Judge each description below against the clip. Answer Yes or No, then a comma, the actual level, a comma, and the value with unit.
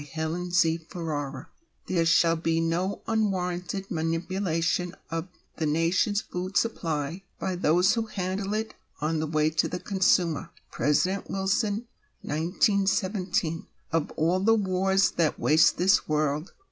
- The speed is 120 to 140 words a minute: Yes, slow, 135 wpm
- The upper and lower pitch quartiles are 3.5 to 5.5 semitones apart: No, average, 3.1 semitones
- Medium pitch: Yes, medium, 175 Hz